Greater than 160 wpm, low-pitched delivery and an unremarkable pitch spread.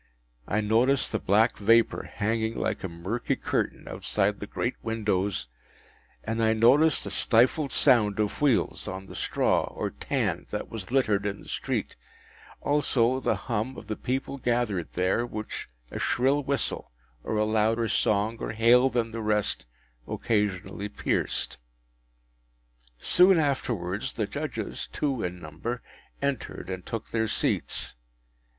No: average, 145 wpm; low, 110 Hz; average, 3.2 semitones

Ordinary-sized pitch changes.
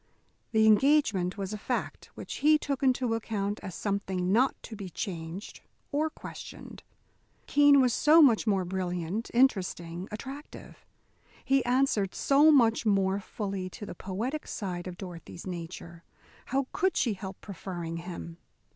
No: wide, 6.0 semitones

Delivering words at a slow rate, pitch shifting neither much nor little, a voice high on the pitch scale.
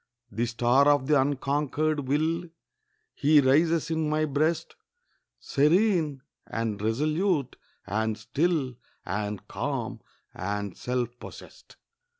No: slow, 105 wpm; average, 4.7 semitones; medium, 140 Hz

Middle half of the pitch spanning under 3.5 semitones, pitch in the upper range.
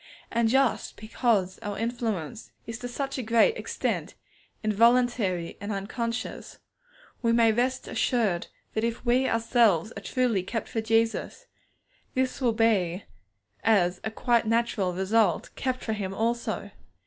Yes: average, 2.7 semitones; high, 225 Hz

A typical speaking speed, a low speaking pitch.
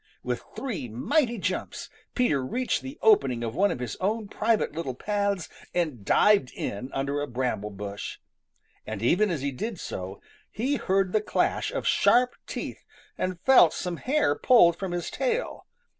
No: average, 165 wpm; medium, 180 Hz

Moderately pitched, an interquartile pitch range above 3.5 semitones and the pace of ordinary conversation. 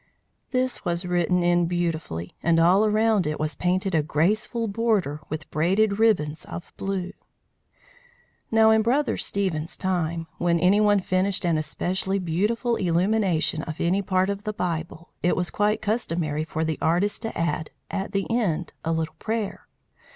Yes: medium, 180 Hz; average, 4.1 semitones; average, 160 wpm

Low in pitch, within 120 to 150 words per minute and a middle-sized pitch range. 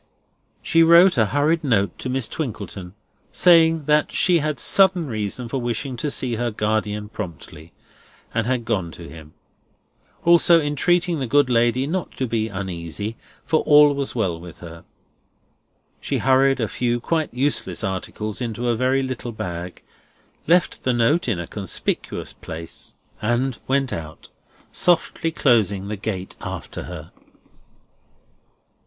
No: low, 120 Hz; average, 145 wpm; wide, 6.1 semitones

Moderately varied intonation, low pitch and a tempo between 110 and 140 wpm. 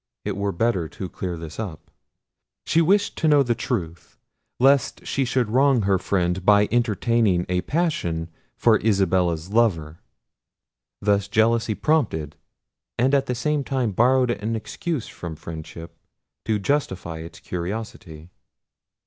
No: wide, 6.1 semitones; low, 105 Hz; slow, 135 wpm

